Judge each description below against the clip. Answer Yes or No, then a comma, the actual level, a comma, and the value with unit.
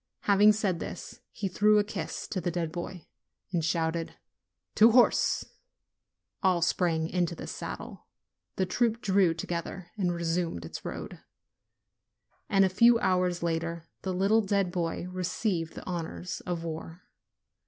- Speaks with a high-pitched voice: No, medium, 180 Hz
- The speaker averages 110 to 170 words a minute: Yes, average, 150 wpm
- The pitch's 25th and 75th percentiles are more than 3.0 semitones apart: No, average, 2.7 semitones